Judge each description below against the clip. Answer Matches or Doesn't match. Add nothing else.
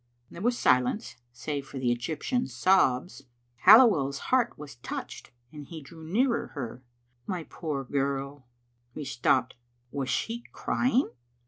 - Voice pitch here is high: Doesn't match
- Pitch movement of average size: Doesn't match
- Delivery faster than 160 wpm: Doesn't match